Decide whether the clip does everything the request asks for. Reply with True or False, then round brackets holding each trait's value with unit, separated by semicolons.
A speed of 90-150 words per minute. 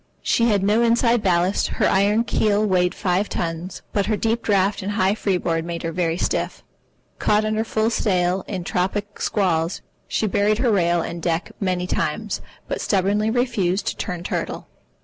False (170 wpm)